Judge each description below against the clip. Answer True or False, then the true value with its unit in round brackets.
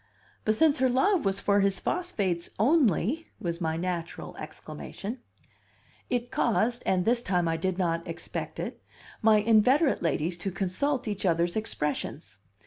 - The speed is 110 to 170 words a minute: True (150 wpm)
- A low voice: False (200 Hz)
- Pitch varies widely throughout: True (6.0 semitones)